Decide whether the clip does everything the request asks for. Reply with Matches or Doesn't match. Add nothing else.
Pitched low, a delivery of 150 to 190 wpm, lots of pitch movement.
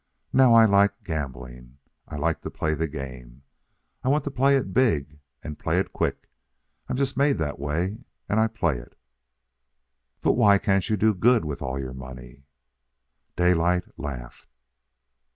Matches